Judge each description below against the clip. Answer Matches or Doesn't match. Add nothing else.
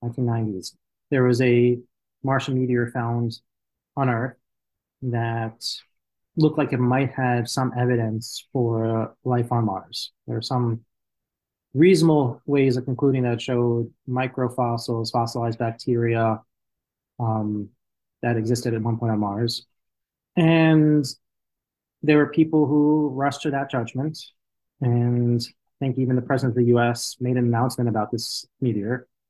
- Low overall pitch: Matches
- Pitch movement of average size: Doesn't match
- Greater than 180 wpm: Doesn't match